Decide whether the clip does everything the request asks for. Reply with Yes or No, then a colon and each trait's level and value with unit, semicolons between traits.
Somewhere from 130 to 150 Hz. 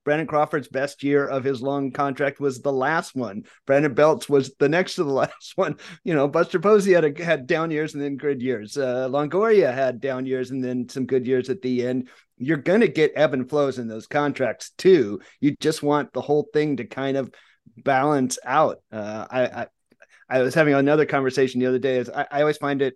Yes: medium, 140 Hz